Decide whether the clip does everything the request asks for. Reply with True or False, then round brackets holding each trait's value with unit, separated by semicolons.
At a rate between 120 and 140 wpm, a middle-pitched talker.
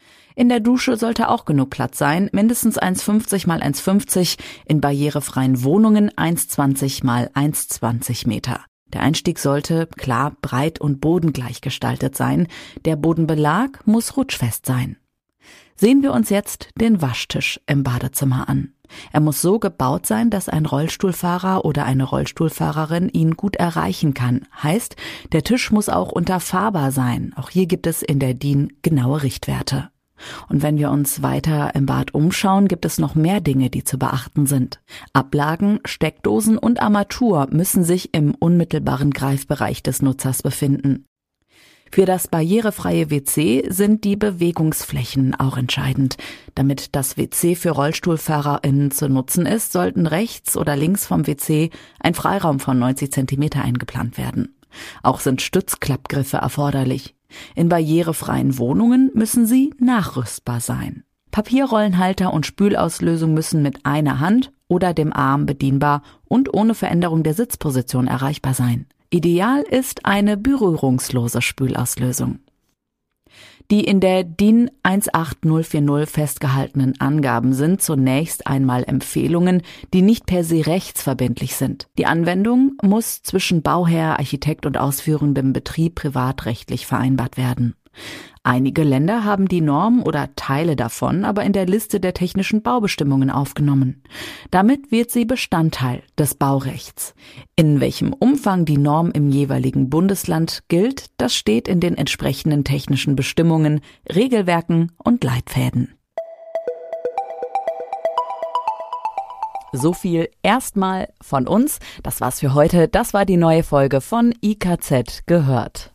True (130 wpm; 160 Hz)